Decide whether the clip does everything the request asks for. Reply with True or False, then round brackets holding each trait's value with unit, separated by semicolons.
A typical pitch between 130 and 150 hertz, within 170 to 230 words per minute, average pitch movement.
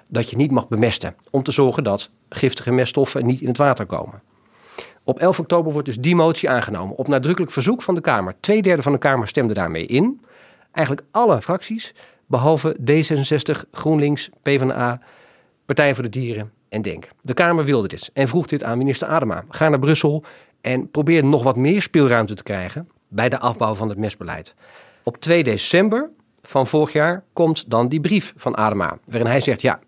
True (140 Hz; 190 wpm; 4.7 semitones)